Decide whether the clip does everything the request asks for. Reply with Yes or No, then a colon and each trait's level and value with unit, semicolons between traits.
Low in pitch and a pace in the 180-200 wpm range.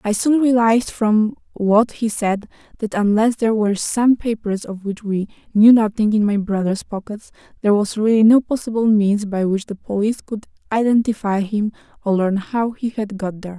No: high, 215 Hz; average, 185 wpm